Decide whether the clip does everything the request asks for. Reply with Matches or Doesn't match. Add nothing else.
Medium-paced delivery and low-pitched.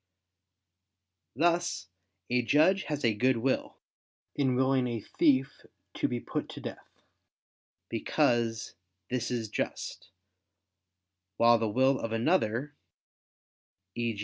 Doesn't match